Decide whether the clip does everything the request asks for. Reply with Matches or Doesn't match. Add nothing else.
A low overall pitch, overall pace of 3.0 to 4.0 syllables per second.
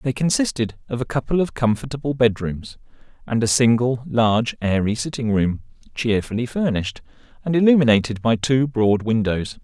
Doesn't match